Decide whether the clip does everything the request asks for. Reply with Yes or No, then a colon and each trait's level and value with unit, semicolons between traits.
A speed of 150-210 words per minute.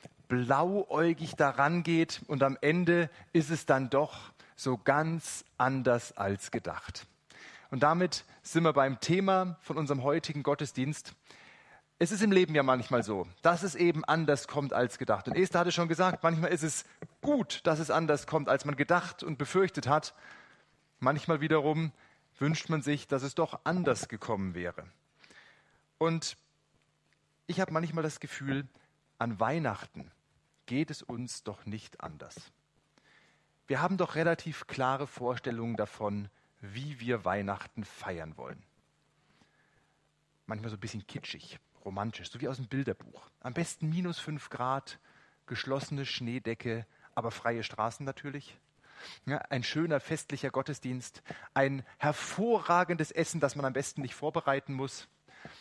No: average, 140 wpm